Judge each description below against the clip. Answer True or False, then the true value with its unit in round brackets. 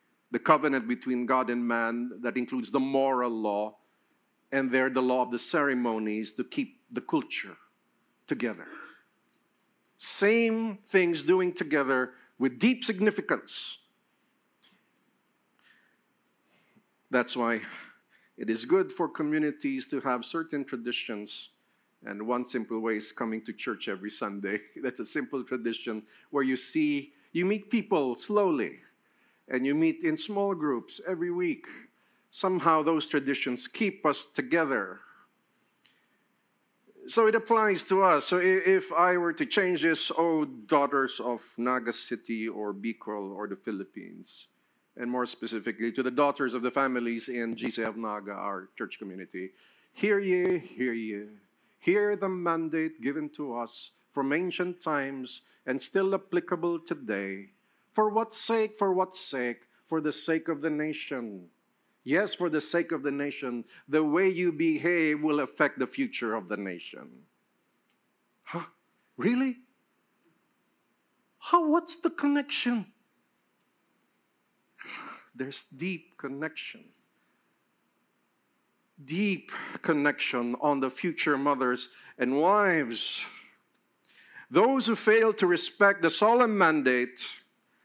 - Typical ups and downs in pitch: False (8.2 semitones)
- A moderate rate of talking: False (125 wpm)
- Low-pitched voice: False (150 Hz)